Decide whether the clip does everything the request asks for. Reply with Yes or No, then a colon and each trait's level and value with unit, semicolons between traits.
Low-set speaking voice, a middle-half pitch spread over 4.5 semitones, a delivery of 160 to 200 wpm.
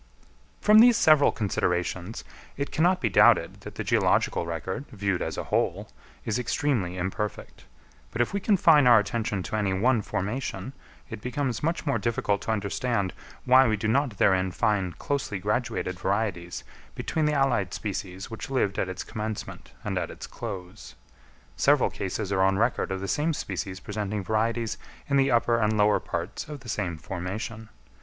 Yes: low, 110 Hz; average, 4.9 semitones; average, 170 wpm